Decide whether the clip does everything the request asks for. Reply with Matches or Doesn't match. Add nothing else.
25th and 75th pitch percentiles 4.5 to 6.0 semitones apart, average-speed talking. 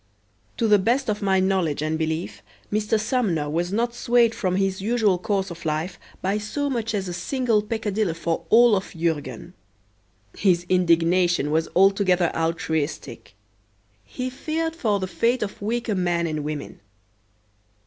Matches